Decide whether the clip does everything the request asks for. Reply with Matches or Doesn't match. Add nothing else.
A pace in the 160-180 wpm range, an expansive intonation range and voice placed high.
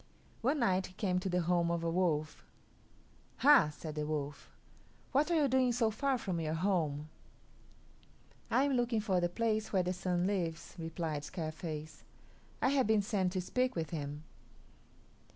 Doesn't match